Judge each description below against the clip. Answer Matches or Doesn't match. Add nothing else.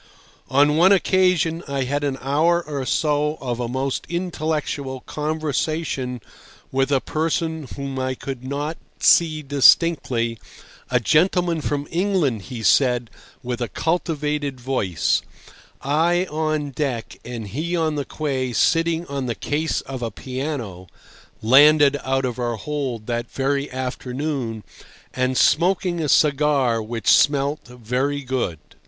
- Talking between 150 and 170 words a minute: Doesn't match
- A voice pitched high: Doesn't match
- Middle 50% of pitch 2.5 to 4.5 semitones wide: Matches